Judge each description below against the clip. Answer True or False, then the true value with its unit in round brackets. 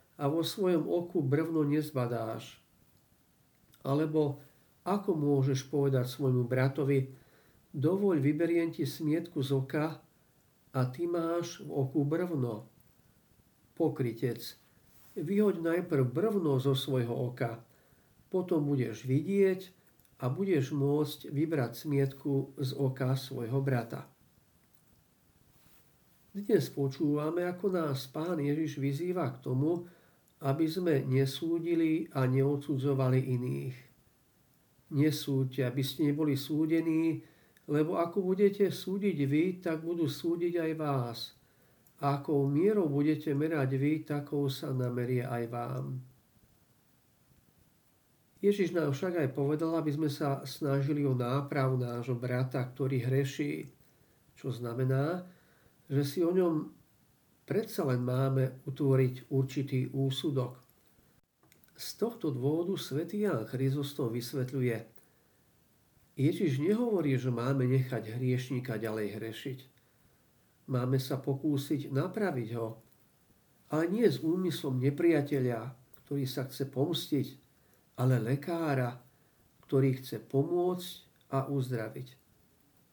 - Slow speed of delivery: True (105 wpm)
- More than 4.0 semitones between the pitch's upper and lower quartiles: False (3.6 semitones)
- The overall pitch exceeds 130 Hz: True (140 Hz)